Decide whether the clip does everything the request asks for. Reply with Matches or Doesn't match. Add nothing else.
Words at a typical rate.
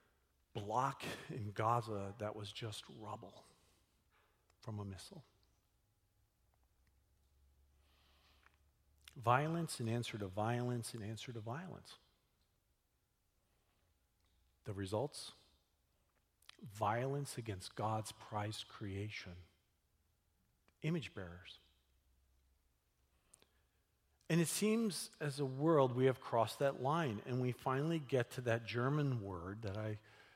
Doesn't match